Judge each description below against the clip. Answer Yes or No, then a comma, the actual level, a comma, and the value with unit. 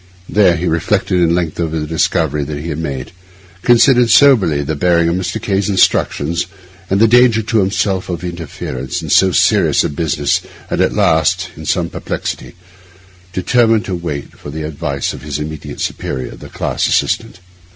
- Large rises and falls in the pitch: No, average, 4.3 semitones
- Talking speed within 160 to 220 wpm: Yes, average, 170 wpm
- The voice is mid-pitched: No, very low, 85 Hz